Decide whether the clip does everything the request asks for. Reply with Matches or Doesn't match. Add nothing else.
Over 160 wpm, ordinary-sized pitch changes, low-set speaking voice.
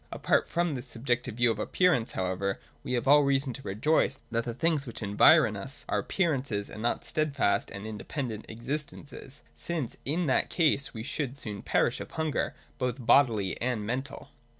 Matches